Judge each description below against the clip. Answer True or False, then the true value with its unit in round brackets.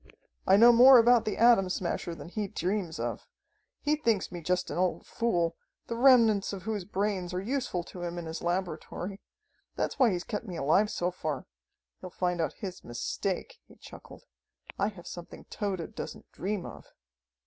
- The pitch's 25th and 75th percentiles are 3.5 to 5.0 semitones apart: True (4.0 semitones)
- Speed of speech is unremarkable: True (180 wpm)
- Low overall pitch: False (190 Hz)